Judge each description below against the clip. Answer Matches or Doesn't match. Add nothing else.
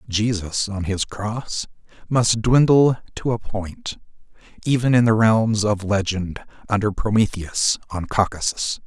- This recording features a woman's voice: Doesn't match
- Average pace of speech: Doesn't match